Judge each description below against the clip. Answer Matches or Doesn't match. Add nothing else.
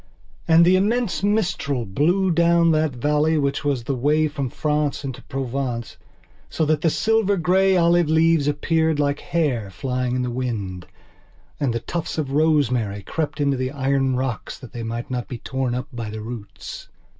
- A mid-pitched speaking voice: Matches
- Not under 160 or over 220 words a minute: Matches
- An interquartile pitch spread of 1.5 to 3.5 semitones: Doesn't match